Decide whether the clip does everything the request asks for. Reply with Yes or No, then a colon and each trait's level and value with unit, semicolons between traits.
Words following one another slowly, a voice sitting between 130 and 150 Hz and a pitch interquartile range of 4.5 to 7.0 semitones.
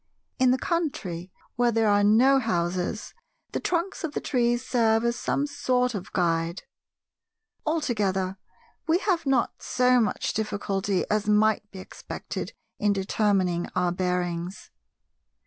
No: slow, 130 wpm; high, 215 Hz; average, 5.1 semitones